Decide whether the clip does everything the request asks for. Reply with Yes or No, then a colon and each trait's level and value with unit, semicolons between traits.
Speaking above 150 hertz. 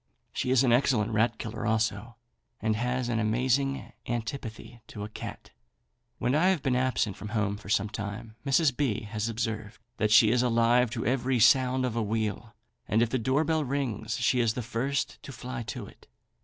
No: low, 115 Hz